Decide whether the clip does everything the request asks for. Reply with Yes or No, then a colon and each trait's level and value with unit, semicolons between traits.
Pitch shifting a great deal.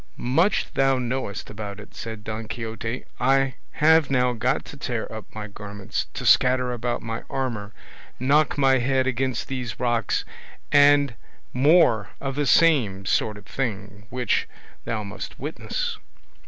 No: average, 3.8 semitones